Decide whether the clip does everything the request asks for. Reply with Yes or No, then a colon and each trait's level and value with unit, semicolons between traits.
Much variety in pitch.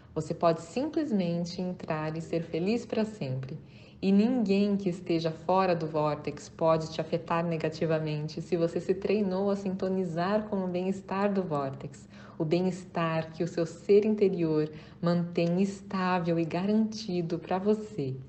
No: average, 3.1 semitones